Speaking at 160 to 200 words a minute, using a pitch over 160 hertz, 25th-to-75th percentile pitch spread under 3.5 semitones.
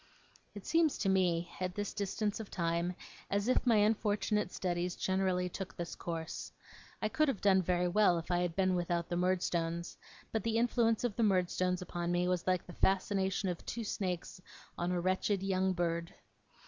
Yes: average, 185 wpm; medium, 185 Hz; average, 2.7 semitones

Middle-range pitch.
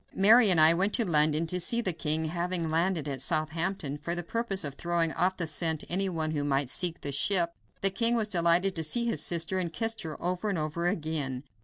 Yes: medium, 170 Hz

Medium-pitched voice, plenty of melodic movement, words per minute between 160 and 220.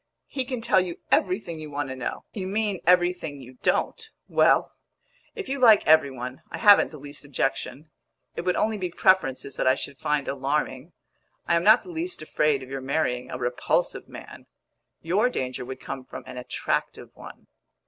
Yes: medium, 155 Hz; wide, 6.7 semitones; average, 185 wpm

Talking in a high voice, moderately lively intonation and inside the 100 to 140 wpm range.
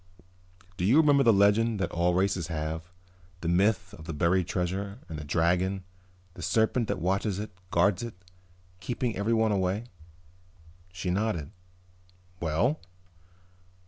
No: very low, 95 Hz; average, 3.9 semitones; slow, 135 wpm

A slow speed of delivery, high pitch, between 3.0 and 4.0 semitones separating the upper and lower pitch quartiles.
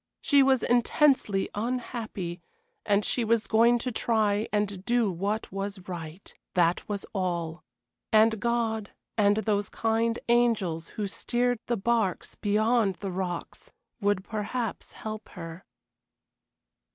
Yes: slow, 125 wpm; high, 215 Hz; average, 3.3 semitones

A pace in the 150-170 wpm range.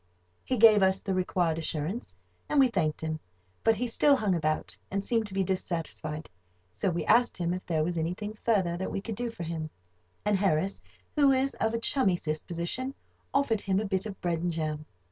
No: average, 200 wpm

